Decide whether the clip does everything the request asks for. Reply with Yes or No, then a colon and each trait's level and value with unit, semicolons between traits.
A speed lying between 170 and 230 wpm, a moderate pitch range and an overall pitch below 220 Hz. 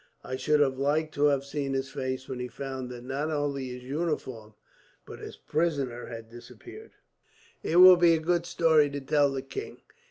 Yes: average, 190 wpm; average, 3.3 semitones; medium, 140 Hz